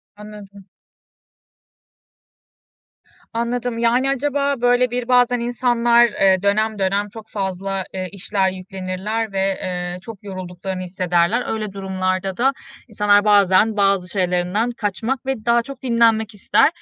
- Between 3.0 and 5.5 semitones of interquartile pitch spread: Yes, average, 3.8 semitones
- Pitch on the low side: No, high, 205 Hz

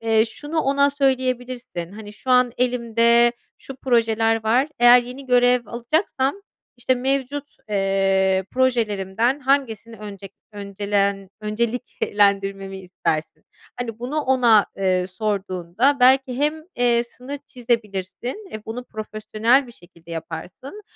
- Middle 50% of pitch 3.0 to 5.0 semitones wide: Yes, average, 4.2 semitones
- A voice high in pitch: Yes, high, 235 Hz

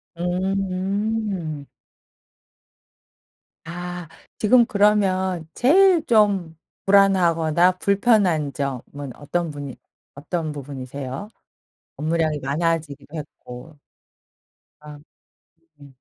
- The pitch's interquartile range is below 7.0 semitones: Yes, average, 5.1 semitones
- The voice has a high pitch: No, medium, 170 Hz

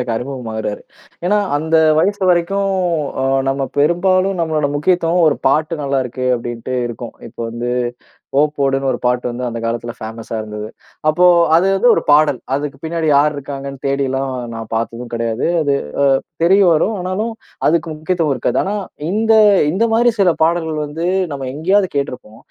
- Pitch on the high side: No, medium, 145 Hz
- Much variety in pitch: Yes, wide, 5.7 semitones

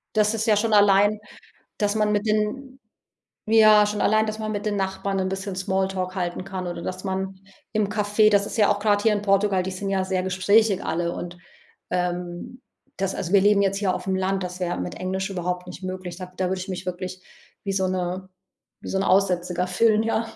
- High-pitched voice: Yes, high, 195 Hz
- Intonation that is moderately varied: No, narrow, 2.2 semitones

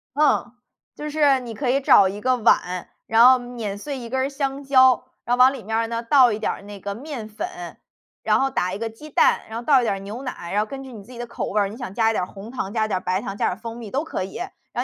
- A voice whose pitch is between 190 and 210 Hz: No, high, 235 Hz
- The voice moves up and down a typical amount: Yes, average, 4.1 semitones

